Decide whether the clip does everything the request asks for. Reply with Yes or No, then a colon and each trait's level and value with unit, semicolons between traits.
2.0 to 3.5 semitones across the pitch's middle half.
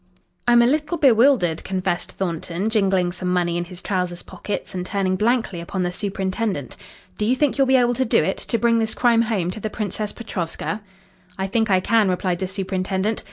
No: average, 4.0 semitones